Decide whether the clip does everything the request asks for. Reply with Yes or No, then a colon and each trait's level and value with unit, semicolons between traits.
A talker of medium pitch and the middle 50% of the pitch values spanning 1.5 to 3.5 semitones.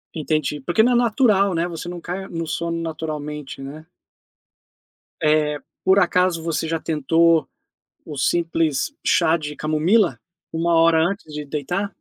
Yes: medium, 165 Hz; narrow, 2.4 semitones